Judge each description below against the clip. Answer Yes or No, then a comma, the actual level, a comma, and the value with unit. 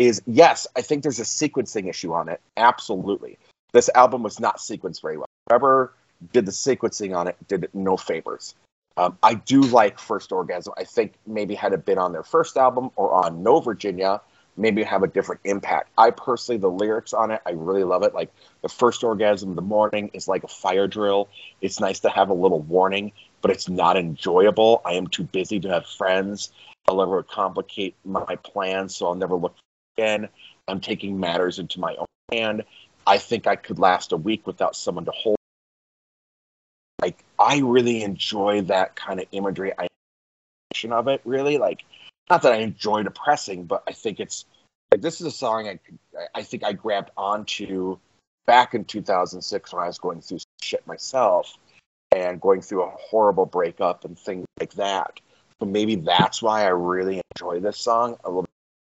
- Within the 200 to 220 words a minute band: No, average, 190 wpm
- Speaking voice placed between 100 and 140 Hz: Yes, low, 105 Hz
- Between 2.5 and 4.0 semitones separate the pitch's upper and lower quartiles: No, average, 4.6 semitones